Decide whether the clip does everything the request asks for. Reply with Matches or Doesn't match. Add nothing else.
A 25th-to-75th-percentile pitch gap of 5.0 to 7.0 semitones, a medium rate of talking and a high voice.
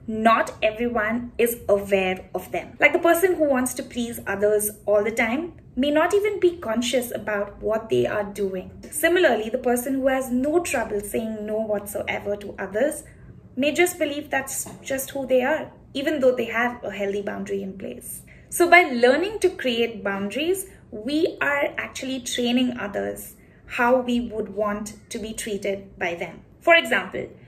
Matches